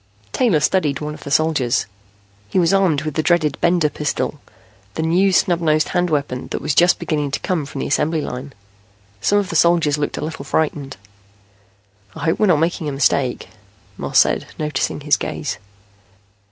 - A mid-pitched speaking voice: Yes, medium, 155 Hz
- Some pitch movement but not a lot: Yes, average, 3.2 semitones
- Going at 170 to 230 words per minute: Yes, average, 180 wpm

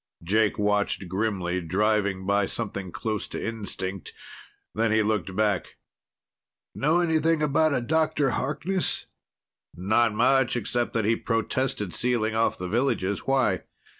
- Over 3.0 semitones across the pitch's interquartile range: Yes, average, 4.6 semitones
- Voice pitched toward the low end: Yes, low, 110 Hz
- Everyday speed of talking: No, slow, 130 wpm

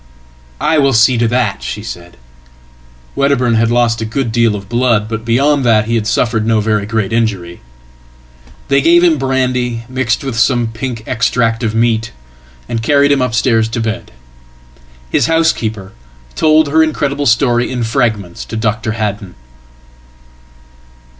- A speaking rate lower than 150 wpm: Yes, average, 140 wpm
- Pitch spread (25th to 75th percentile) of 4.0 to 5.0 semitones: No, average, 2.9 semitones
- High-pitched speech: No, low, 115 Hz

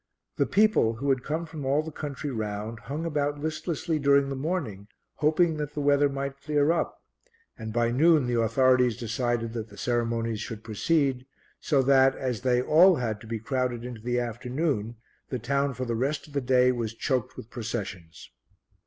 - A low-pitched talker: Yes, low, 130 Hz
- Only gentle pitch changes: No, average, 3.9 semitones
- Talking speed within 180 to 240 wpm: Yes, average, 185 wpm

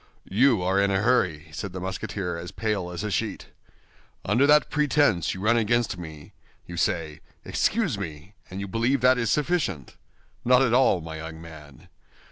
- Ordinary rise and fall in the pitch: No, wide, 6.3 semitones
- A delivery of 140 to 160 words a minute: No, average, 175 wpm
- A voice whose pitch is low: Yes, low, 100 Hz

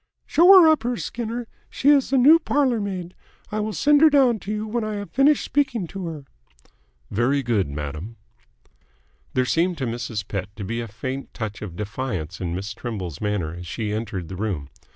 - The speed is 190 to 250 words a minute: Yes, average, 195 wpm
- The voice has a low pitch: Yes, low, 130 Hz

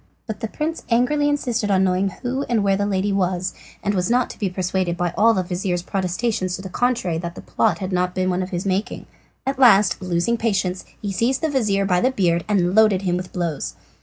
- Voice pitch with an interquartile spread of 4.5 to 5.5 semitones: No, average, 4.0 semitones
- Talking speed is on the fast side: Yes, fast, 225 wpm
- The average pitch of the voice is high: Yes, high, 195 Hz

